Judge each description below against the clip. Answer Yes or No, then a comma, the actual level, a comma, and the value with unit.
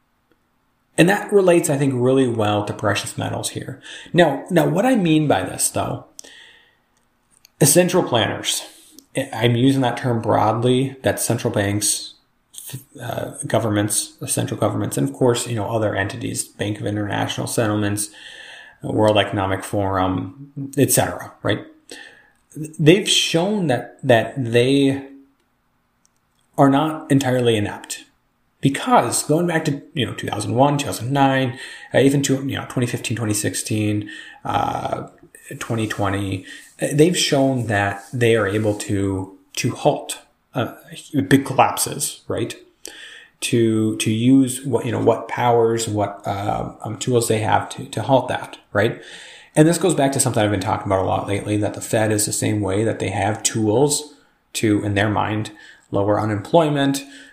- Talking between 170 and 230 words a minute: No, average, 145 wpm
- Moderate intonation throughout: Yes, average, 4.9 semitones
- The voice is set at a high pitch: No, low, 120 Hz